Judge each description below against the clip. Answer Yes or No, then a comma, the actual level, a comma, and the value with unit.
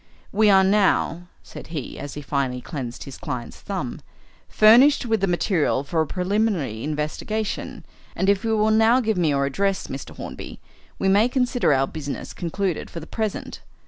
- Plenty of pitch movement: Yes, wide, 6.8 semitones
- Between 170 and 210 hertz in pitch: Yes, medium, 185 Hz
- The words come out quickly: No, average, 175 wpm